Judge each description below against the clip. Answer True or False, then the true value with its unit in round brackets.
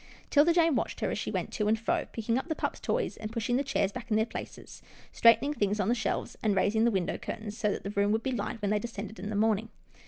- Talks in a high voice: True (220 Hz)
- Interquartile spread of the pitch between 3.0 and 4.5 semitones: False (2.5 semitones)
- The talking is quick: True (275 wpm)